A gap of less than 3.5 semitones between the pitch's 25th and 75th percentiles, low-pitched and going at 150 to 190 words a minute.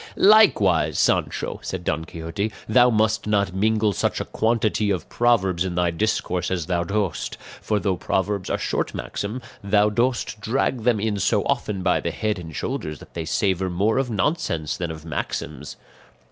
No: average, 3.9 semitones; low, 100 Hz; average, 175 wpm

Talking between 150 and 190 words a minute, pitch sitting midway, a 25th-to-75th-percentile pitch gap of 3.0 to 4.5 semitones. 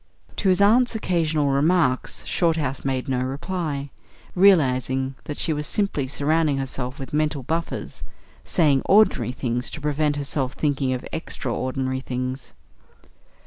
No: slow, 135 wpm; medium, 145 Hz; average, 3.8 semitones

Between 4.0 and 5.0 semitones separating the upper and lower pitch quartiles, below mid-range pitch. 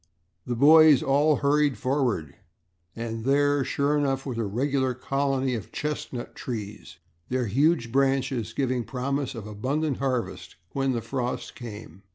No: average, 3.2 semitones; low, 130 Hz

